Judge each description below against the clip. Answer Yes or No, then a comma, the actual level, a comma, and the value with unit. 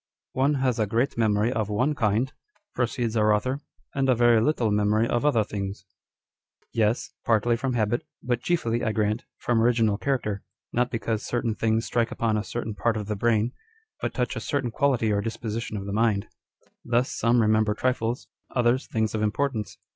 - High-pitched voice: No, low, 115 Hz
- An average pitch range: No, narrow, 2.2 semitones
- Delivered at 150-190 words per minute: Yes, average, 185 wpm